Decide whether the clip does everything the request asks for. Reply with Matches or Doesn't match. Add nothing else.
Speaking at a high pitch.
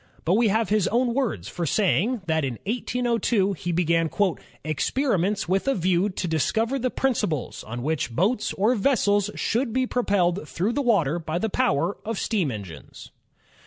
Matches